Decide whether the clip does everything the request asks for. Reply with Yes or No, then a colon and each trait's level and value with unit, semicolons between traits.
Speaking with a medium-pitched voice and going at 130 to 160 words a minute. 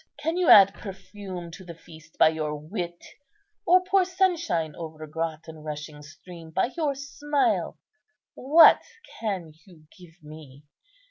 Yes: medium, 175 Hz; average, 140 wpm